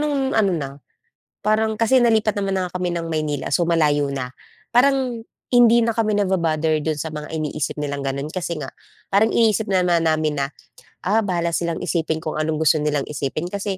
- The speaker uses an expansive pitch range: Yes, wide, 5.8 semitones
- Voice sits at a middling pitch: Yes, medium, 170 Hz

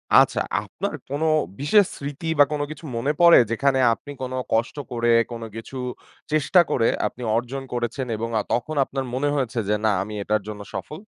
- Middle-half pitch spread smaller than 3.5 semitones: No, average, 3.9 semitones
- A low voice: Yes, low, 130 Hz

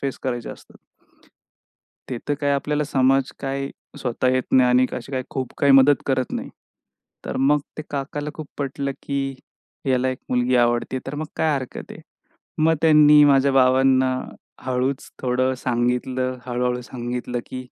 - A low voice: Yes, low, 130 Hz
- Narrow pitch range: Yes, narrow, 1.7 semitones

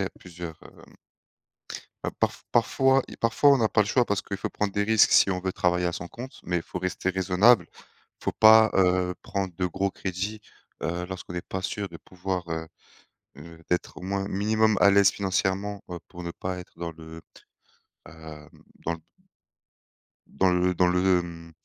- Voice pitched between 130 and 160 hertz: No, very low, 95 Hz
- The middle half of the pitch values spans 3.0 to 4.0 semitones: No, narrow, 2.4 semitones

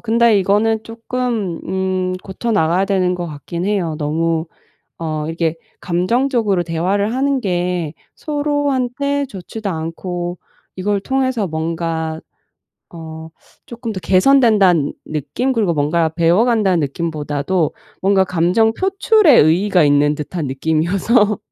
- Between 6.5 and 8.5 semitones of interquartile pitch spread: No, wide, 5.5 semitones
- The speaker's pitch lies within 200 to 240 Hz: No, medium, 185 Hz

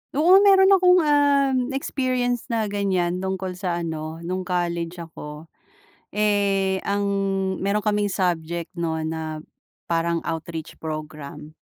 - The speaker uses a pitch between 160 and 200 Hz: Yes, medium, 185 Hz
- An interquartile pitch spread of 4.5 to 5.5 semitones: Yes, average, 4.9 semitones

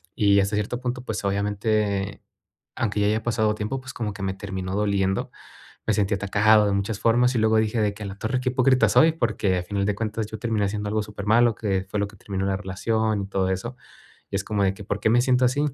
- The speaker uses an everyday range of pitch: No, narrow, 2.2 semitones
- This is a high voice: No, low, 105 Hz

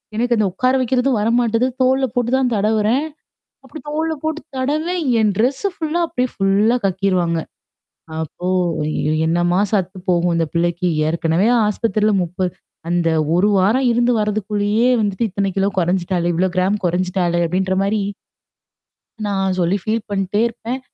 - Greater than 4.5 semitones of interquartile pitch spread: Yes, average, 5.0 semitones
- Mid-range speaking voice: No, high, 205 Hz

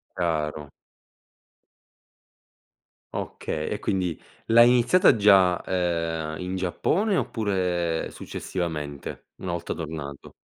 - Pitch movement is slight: No, average, 3.2 semitones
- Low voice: Yes, very low, 90 Hz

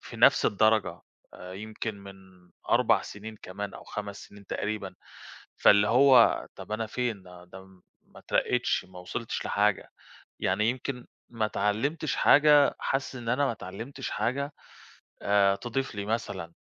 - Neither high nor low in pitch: No, low, 110 Hz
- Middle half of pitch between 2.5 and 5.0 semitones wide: Yes, average, 3.8 semitones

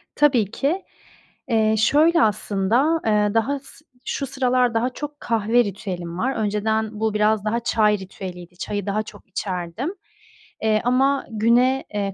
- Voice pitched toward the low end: No, high, 220 Hz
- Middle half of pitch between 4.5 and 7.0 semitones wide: No, average, 3.8 semitones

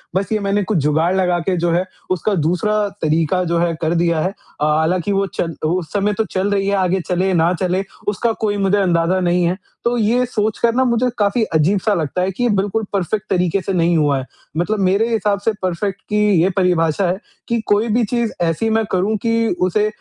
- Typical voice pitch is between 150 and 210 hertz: Yes, high, 190 Hz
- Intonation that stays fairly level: No, average, 3.3 semitones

